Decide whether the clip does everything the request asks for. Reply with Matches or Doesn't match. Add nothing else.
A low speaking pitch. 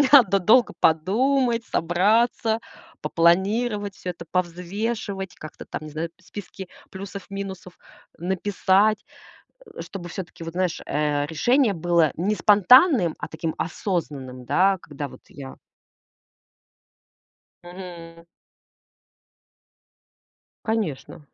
Doesn't match